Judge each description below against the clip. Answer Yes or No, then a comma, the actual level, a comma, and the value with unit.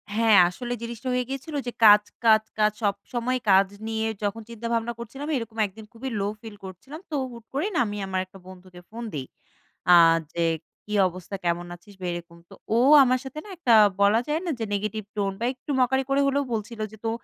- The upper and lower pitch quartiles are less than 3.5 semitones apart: No, average, 4.1 semitones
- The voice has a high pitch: Yes, high, 225 Hz